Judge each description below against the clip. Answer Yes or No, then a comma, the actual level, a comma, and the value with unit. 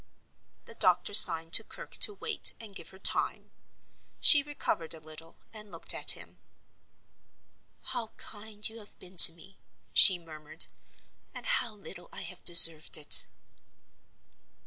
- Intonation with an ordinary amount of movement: Yes, average, 5.0 semitones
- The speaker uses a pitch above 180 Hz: Yes, high, 190 Hz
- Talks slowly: No, average, 145 wpm